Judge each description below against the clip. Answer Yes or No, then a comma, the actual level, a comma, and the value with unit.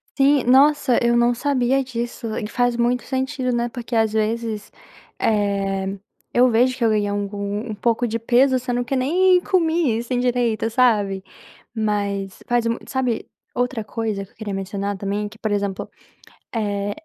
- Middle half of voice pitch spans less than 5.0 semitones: Yes, average, 3.3 semitones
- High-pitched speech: Yes, high, 230 Hz